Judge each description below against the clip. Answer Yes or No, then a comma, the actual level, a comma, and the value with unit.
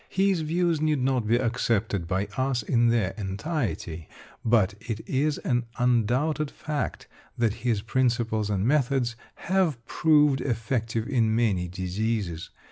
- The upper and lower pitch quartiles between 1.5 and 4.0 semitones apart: No, average, 4.5 semitones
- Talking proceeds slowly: Yes, slow, 130 wpm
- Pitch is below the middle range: Yes, low, 120 Hz